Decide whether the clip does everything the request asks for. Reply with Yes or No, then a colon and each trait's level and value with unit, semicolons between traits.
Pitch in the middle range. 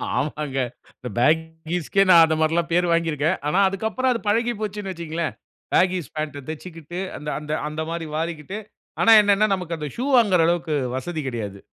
Yes: medium, 165 Hz